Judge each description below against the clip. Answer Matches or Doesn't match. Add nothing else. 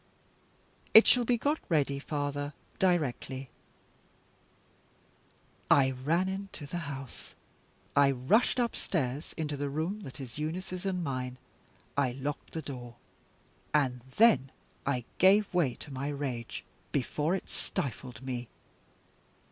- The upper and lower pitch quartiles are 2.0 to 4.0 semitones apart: Doesn't match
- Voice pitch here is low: Doesn't match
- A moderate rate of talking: Doesn't match